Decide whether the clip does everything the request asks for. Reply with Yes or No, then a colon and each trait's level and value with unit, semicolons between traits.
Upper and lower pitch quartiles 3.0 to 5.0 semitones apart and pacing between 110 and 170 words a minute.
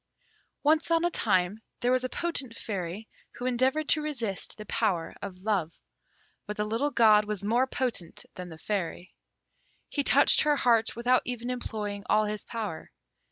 Yes: average, 4.0 semitones; average, 165 wpm